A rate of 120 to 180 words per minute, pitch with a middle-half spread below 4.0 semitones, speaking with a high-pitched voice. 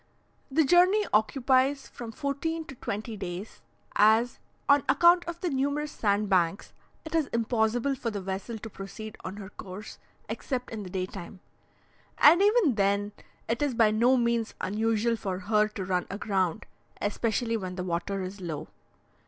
No: average, 160 wpm; average, 5.3 semitones; high, 220 Hz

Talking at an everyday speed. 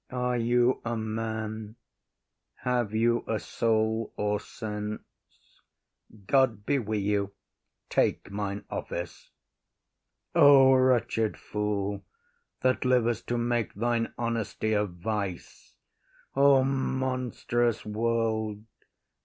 No: slow, 95 wpm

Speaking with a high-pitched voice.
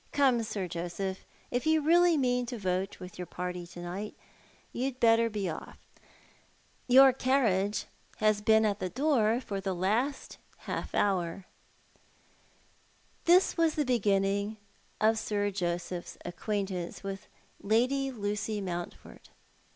Yes: high, 210 Hz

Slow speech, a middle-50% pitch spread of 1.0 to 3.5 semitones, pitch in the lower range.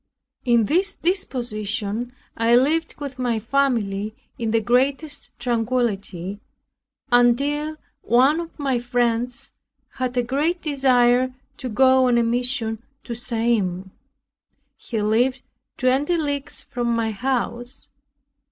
No: slow, 115 wpm; average, 2.9 semitones; high, 245 Hz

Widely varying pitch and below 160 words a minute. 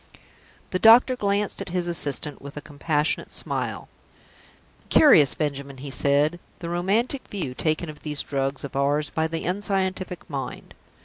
No: average, 4.8 semitones; average, 145 wpm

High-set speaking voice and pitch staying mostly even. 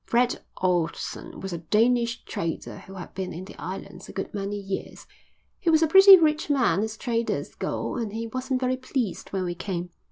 No: high, 220 Hz; wide, 5.4 semitones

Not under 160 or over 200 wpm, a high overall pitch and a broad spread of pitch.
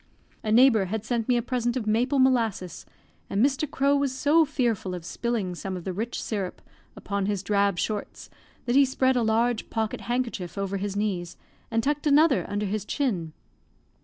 No: average, 185 wpm; high, 225 Hz; average, 4.5 semitones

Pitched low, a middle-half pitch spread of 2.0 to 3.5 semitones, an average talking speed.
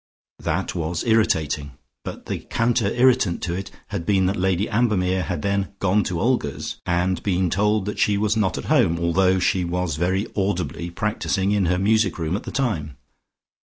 Yes: very low, 95 Hz; average, 3.1 semitones; average, 180 wpm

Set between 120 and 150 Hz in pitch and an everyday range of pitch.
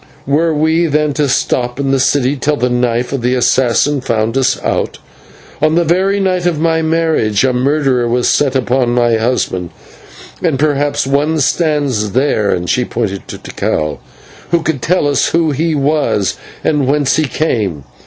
Yes: medium, 140 Hz; average, 4.1 semitones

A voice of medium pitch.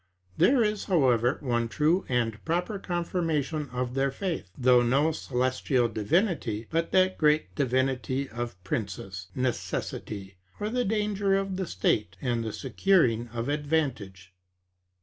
No: low, 130 Hz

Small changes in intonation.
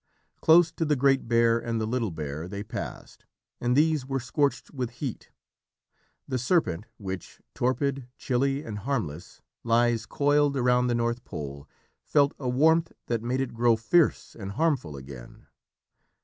No: average, 4.0 semitones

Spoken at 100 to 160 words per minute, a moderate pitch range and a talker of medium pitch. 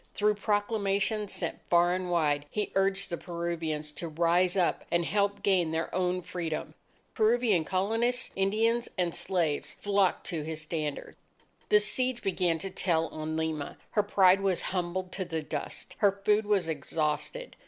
Yes: average, 155 wpm; average, 3.8 semitones; medium, 180 Hz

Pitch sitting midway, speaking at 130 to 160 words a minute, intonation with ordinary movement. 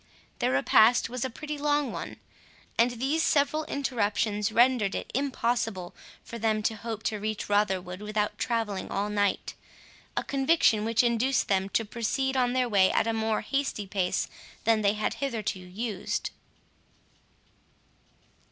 No: high, 225 Hz; average, 145 wpm; average, 3.6 semitones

